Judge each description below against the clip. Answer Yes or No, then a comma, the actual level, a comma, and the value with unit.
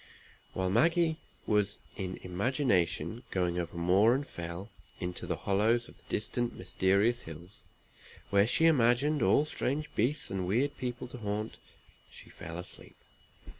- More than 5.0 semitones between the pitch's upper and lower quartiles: Yes, wide, 5.4 semitones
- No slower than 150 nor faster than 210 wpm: No, average, 140 wpm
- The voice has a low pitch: Yes, low, 105 Hz